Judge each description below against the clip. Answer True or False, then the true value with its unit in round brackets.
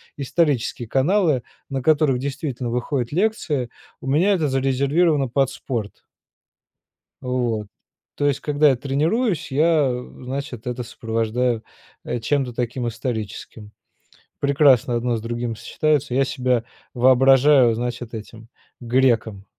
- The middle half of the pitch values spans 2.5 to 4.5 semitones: True (3.2 semitones)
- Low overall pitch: True (130 Hz)